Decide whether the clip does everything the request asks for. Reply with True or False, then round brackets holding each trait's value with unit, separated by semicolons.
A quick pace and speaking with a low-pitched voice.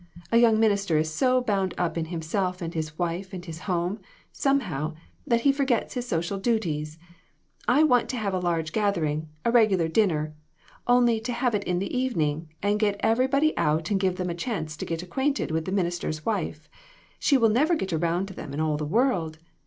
False (210 wpm; 190 Hz)